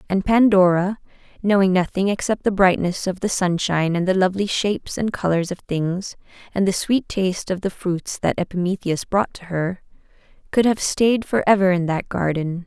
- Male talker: No, female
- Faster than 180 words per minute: No, average, 175 wpm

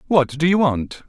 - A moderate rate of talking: No, fast, 220 wpm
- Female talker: No, male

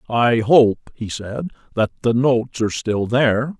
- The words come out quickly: No, average, 165 wpm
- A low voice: Yes, low, 120 Hz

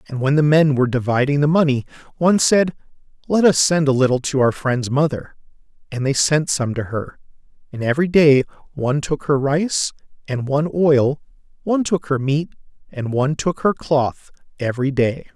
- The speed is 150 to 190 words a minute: Yes, average, 180 wpm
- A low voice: No, medium, 145 Hz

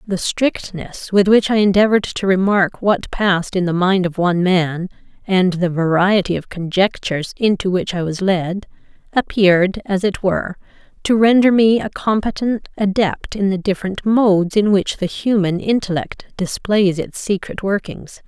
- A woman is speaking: Yes, female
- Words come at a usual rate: Yes, average, 160 wpm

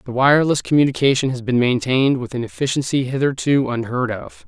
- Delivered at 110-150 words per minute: No, average, 160 wpm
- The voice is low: Yes, low, 130 Hz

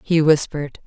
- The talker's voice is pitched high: No, medium, 150 Hz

